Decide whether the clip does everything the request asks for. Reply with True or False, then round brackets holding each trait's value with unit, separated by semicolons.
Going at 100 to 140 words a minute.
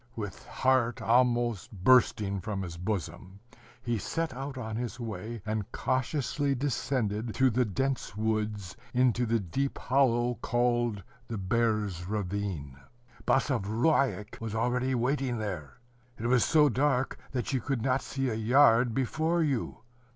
True (135 wpm)